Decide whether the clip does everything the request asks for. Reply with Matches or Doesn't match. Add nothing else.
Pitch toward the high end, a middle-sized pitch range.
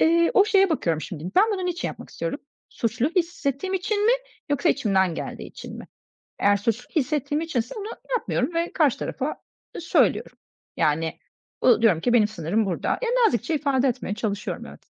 Doesn't match